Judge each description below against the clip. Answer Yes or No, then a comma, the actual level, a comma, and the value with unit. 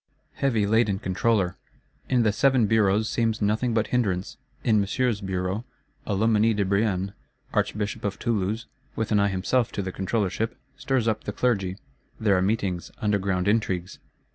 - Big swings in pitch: No, average, 2.7 semitones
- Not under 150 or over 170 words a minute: Yes, average, 155 wpm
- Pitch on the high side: No, low, 105 Hz